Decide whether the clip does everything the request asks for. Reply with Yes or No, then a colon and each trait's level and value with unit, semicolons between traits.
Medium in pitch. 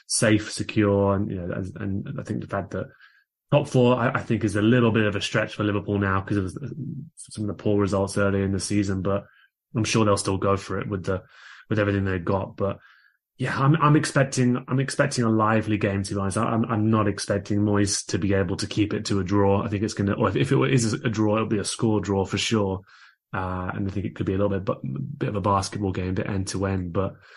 No: low, 105 Hz